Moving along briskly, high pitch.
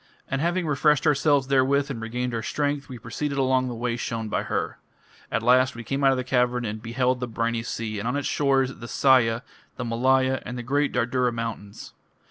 No: fast, 210 wpm; low, 125 Hz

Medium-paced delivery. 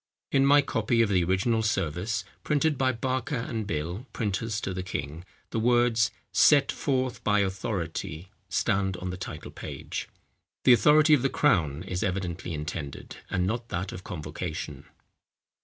Yes: average, 155 wpm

